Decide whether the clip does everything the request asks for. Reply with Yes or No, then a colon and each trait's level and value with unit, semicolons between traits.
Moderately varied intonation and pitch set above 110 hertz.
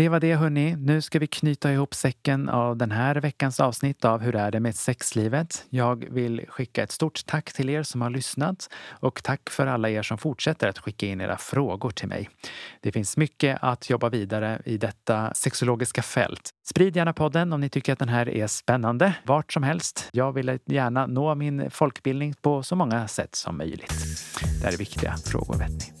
Yes: average, 4.7 semitones; low, 130 Hz